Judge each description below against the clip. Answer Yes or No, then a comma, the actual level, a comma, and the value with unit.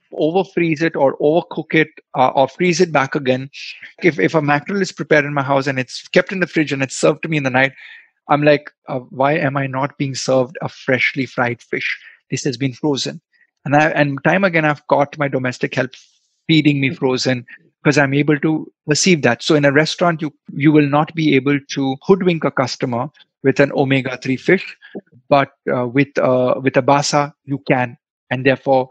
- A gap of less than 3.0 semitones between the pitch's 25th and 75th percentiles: Yes, narrow, 2.6 semitones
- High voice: No, medium, 145 Hz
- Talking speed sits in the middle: No, fast, 210 wpm